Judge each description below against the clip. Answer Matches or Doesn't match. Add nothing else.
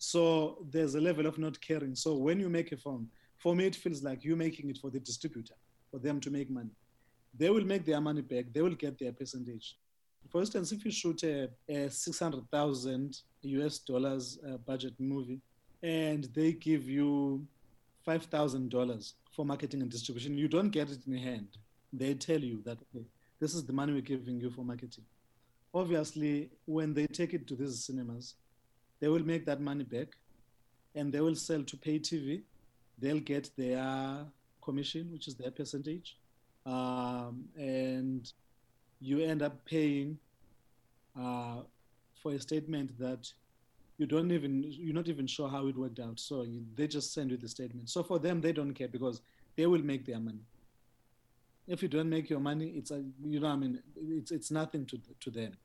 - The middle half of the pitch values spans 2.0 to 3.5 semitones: Doesn't match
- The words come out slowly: Doesn't match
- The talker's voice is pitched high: Doesn't match